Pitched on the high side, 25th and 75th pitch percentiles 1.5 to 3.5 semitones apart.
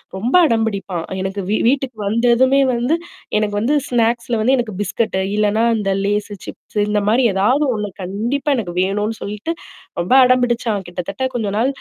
Yes: high, 220 Hz; average, 3.1 semitones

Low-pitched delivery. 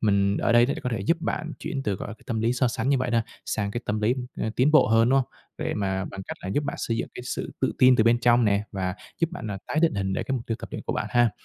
Yes: low, 115 Hz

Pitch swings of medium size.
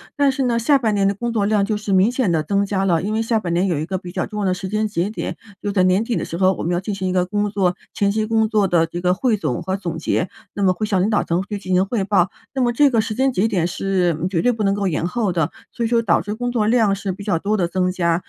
Yes: average, 3.1 semitones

